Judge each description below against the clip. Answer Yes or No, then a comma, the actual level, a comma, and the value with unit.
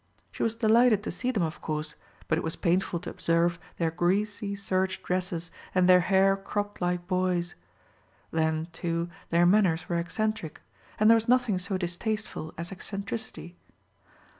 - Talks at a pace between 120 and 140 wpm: No, average, 160 wpm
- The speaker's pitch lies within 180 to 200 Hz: Yes, medium, 185 Hz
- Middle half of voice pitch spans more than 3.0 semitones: Yes, average, 3.4 semitones